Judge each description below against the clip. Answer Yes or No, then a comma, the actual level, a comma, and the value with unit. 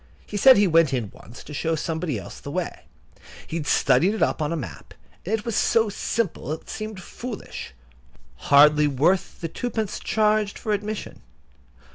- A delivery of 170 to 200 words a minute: Yes, average, 175 wpm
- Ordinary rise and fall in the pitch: No, wide, 6.9 semitones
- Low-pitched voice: No, medium, 165 Hz